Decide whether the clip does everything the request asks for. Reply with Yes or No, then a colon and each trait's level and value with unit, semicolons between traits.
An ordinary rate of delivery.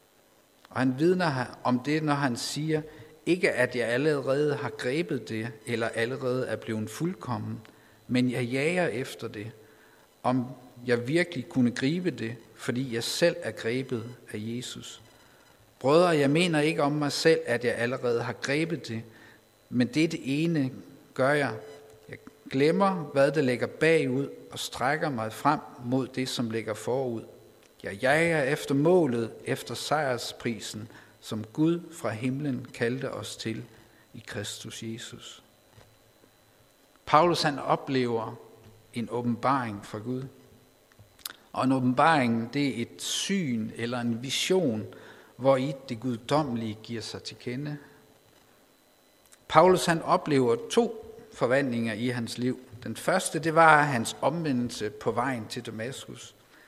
No: slow, 140 wpm